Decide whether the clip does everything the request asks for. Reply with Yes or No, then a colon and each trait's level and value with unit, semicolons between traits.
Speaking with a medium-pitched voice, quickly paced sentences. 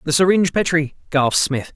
No: medium, 155 Hz; average, 170 wpm